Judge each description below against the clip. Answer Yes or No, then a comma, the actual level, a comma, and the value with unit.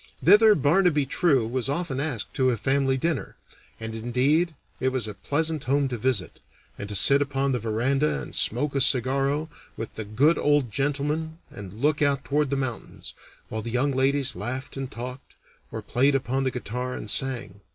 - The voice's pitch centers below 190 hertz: Yes, low, 135 Hz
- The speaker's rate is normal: Yes, average, 185 wpm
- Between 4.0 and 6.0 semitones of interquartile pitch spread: No, average, 2.9 semitones